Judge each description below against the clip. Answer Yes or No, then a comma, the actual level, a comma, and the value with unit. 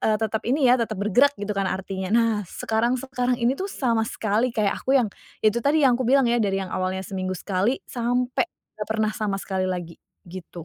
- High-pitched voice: Yes, high, 220 Hz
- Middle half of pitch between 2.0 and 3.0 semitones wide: No, average, 4.3 semitones